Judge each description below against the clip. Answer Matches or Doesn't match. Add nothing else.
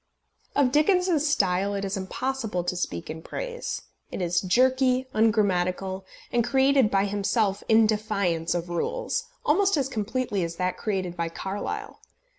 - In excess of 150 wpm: Doesn't match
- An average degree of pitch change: Doesn't match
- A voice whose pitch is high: Matches